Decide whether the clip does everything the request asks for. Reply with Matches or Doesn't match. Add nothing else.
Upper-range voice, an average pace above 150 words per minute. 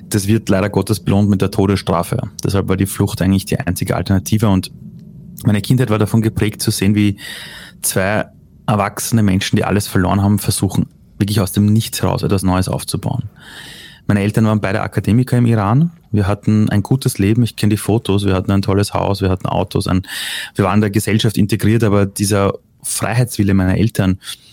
Doesn't match